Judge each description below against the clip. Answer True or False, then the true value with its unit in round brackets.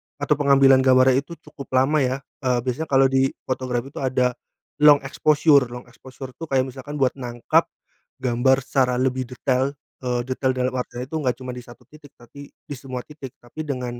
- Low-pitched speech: True (130 Hz)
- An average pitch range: False (1.8 semitones)